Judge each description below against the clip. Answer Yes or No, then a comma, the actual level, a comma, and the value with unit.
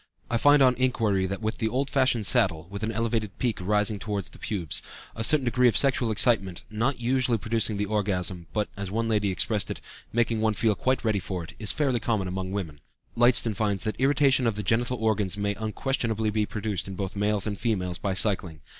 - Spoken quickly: Yes, fast, 210 wpm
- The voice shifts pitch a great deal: No, average, 3.0 semitones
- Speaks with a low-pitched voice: Yes, low, 110 Hz